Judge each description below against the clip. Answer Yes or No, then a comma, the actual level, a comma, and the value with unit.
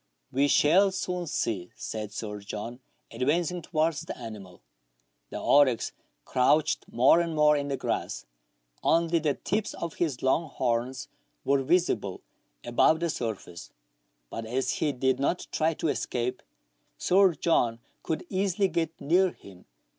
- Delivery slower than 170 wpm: Yes, average, 145 wpm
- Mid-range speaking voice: Yes, medium, 145 Hz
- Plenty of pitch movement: Yes, wide, 6.0 semitones